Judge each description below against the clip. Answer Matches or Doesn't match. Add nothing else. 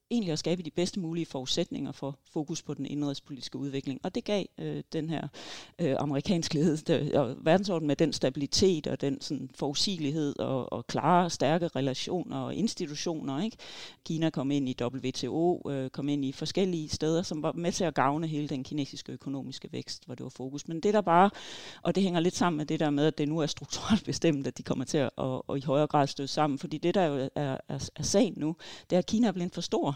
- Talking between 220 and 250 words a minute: Matches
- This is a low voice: Doesn't match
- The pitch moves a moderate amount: Matches